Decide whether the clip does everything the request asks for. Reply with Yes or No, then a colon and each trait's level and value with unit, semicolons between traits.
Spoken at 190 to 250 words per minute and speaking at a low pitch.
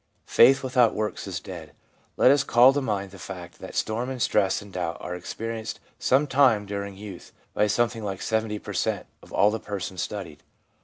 Yes: average, 195 wpm; low, 105 Hz